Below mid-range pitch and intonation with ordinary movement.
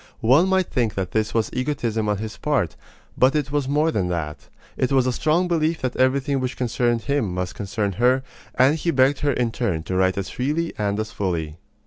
No: low, 125 Hz; wide, 5.7 semitones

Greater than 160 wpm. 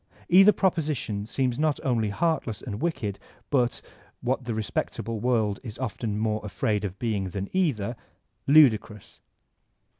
No: average, 150 wpm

